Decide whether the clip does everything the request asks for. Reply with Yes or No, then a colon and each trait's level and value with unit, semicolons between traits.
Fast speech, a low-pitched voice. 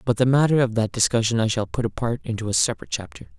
Yes: fast, 250 wpm; low, 115 Hz